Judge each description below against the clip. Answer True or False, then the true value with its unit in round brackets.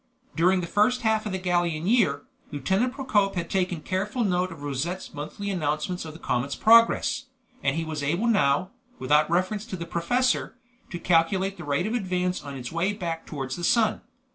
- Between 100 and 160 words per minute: False (190 wpm)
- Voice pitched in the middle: True (180 Hz)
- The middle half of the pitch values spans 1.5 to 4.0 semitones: False (4.7 semitones)